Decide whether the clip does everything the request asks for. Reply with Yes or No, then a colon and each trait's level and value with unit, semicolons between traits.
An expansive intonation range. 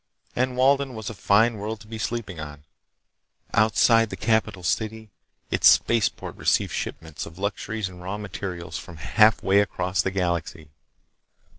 No: average, 3.6 semitones